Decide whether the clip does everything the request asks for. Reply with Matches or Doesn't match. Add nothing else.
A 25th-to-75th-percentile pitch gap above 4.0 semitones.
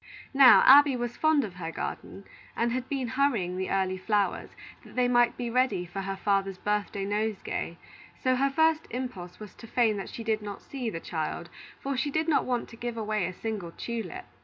Matches